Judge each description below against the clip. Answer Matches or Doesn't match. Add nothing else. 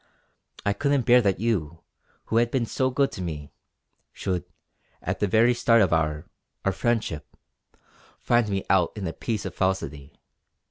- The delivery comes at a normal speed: Matches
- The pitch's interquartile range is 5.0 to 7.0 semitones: Matches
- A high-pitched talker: Doesn't match